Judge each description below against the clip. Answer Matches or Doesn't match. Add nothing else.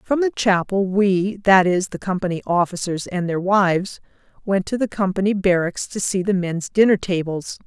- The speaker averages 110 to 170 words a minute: Matches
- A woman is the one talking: Matches